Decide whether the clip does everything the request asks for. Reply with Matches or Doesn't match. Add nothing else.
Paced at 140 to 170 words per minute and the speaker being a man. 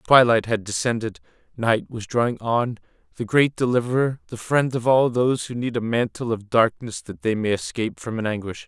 Doesn't match